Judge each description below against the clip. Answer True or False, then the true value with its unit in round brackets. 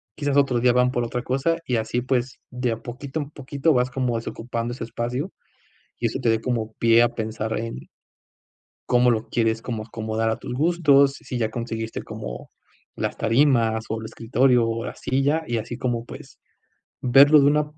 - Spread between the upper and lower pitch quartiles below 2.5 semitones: False (2.9 semitones)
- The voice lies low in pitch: True (120 Hz)